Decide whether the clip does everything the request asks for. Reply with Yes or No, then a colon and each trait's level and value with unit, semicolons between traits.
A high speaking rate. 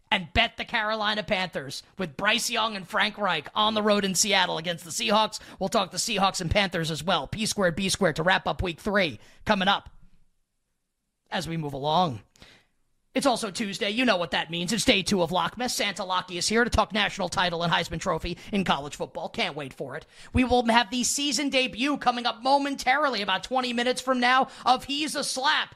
Yes: fast, 210 wpm